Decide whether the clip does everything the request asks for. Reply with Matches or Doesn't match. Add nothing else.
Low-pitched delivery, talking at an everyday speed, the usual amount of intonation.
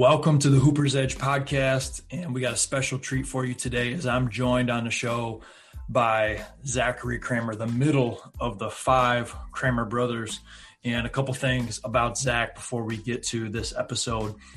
Doesn't match